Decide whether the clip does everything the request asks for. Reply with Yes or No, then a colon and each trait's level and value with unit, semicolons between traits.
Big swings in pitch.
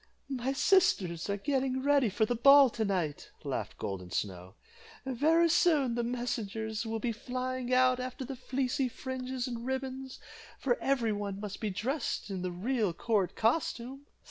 No: average, 4.0 semitones